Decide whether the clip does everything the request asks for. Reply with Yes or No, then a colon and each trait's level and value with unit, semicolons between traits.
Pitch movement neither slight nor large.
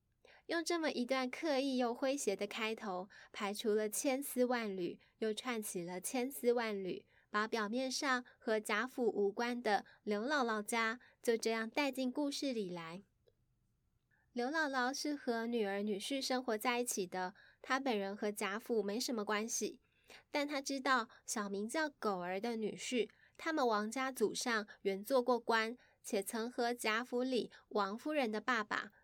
Yes: average, 3.6 semitones